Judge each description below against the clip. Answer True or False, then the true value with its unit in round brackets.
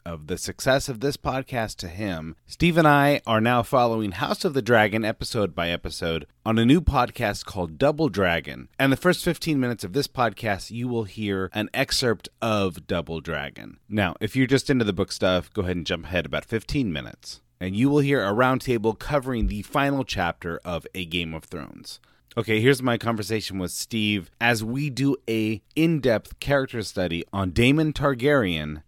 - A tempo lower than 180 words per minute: False (190 wpm)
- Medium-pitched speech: False (110 Hz)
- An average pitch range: False (6.5 semitones)